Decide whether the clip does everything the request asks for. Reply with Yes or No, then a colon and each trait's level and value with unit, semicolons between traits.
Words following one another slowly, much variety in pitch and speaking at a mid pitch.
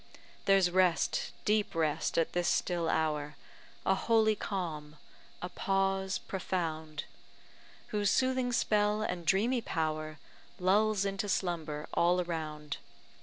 No: slow, 115 wpm; average, 4.1 semitones; medium, 180 Hz